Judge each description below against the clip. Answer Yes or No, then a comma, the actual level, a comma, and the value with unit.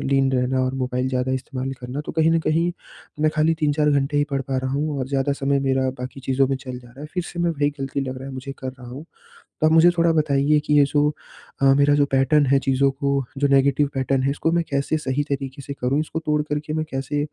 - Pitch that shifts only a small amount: Yes, narrow, 2.1 semitones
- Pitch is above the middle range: No, medium, 140 Hz